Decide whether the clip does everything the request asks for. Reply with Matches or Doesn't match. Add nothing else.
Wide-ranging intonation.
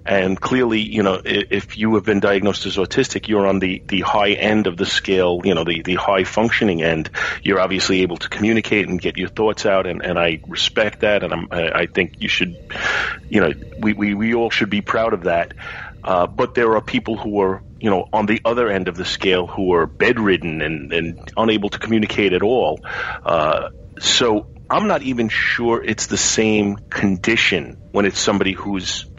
Doesn't match